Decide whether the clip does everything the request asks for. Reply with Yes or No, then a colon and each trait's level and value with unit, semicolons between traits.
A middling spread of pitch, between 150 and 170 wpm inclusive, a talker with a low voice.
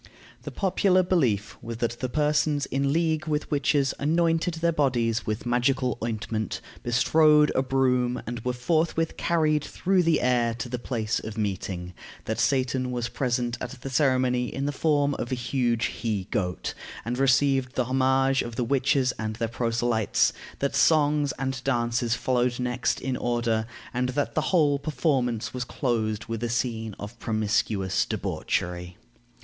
Yes: average, 3.5 semitones; average, 160 wpm; low, 125 Hz